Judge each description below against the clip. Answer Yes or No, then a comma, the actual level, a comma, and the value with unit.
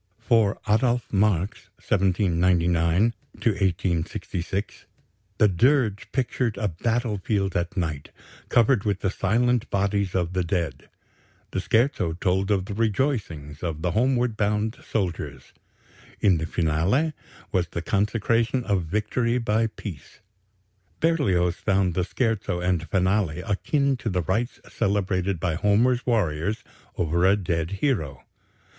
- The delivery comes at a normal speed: No, slow, 125 wpm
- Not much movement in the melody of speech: No, average, 4.5 semitones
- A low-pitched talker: Yes, low, 100 Hz